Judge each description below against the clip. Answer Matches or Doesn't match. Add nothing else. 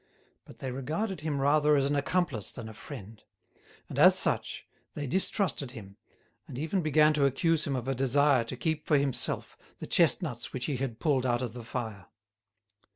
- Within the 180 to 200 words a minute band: Matches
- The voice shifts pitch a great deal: Doesn't match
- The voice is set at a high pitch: Doesn't match